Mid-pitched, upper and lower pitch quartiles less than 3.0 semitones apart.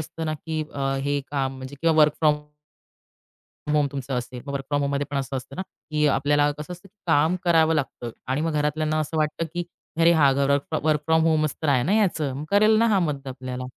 Yes: medium, 150 Hz; narrow, 2.6 semitones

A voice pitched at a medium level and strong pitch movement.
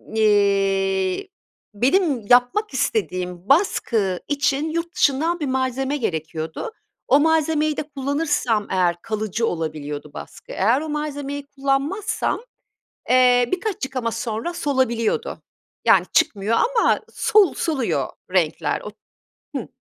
No: very high, 260 Hz; wide, 6.6 semitones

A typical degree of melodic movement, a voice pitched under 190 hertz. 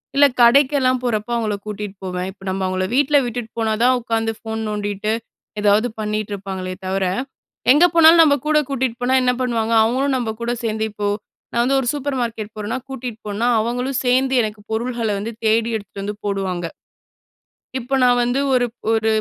No: average, 3.4 semitones; high, 230 Hz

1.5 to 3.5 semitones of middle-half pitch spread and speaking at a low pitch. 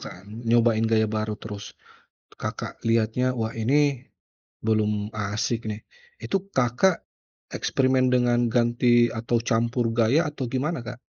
Yes: narrow, 2.4 semitones; low, 120 Hz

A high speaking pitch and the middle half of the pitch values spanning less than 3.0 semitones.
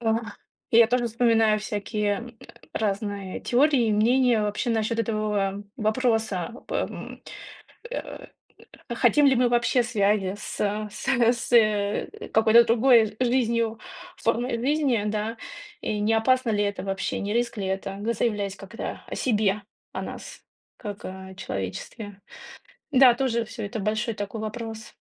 Yes: high, 220 Hz; narrow, 2.6 semitones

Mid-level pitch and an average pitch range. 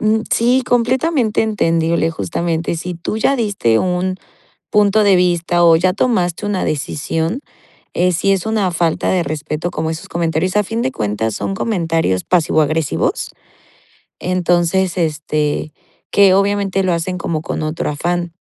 Yes: medium, 175 Hz; average, 3.5 semitones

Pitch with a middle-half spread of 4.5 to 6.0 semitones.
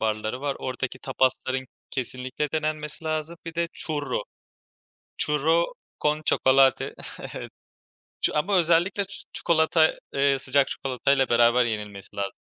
No: average, 3.5 semitones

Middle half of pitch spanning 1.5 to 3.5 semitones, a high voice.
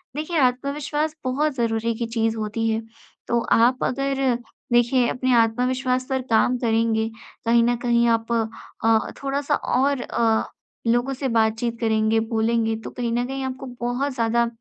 Yes: narrow, 2.5 semitones; high, 240 Hz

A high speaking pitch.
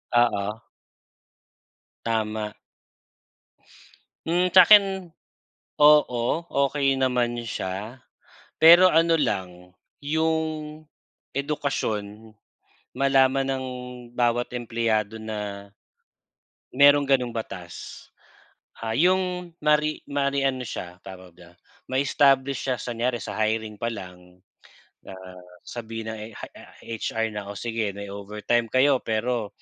No: low, 120 Hz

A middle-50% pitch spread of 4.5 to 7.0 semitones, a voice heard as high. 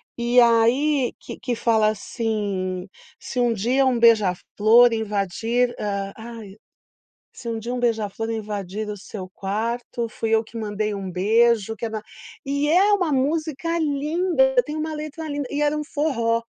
Yes: average, 4.8 semitones; high, 230 Hz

